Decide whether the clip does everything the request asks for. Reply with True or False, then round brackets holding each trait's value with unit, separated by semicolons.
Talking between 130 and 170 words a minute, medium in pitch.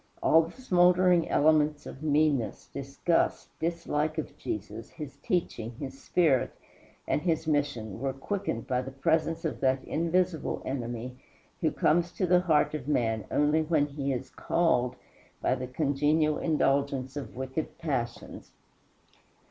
True (140 wpm; 150 Hz)